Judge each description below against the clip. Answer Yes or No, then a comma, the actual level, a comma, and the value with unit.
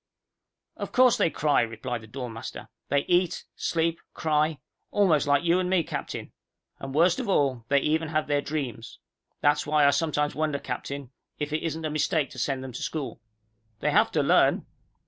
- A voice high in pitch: No, medium, 150 Hz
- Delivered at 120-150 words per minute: No, average, 185 wpm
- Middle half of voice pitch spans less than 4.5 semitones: Yes, average, 2.8 semitones